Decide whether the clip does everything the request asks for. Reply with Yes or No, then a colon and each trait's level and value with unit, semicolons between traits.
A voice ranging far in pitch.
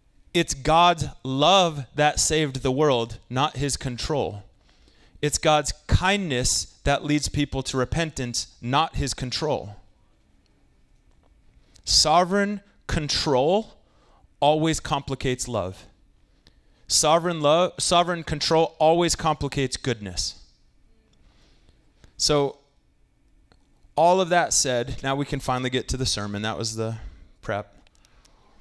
Yes: wide, 5.8 semitones